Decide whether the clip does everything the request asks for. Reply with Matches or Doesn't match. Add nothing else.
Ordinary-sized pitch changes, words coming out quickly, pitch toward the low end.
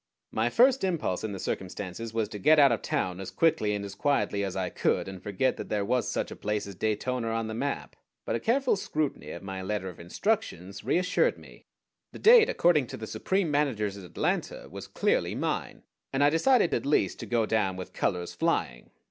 Doesn't match